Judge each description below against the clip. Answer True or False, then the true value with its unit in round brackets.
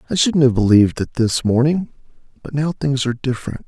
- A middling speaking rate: True (195 wpm)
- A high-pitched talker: False (130 Hz)